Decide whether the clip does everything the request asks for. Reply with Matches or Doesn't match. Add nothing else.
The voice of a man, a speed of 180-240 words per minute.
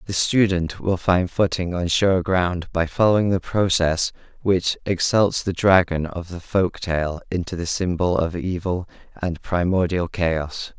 Doesn't match